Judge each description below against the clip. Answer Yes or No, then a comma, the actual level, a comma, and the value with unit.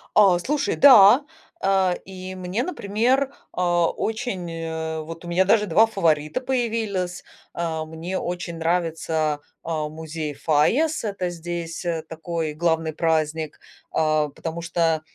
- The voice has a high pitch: No, medium, 170 Hz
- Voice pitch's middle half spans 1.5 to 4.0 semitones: Yes, average, 3.4 semitones